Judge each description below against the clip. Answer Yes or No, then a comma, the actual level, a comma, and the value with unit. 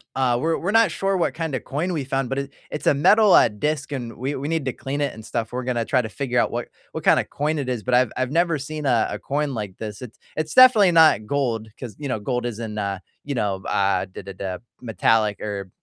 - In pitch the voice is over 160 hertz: No, low, 130 Hz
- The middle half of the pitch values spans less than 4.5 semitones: No, average, 5.2 semitones